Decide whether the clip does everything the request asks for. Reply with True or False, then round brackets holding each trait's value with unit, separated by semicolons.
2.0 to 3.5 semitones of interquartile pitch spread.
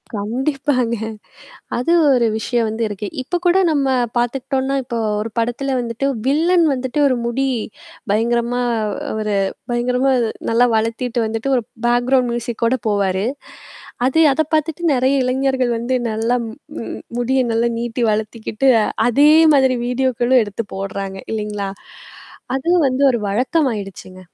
True (2.9 semitones)